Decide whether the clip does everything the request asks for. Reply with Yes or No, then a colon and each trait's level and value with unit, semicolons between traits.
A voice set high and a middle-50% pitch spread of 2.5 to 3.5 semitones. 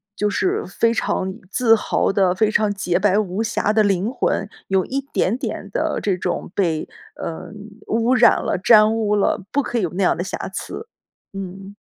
Yes: high, 205 Hz; average, 3.0 semitones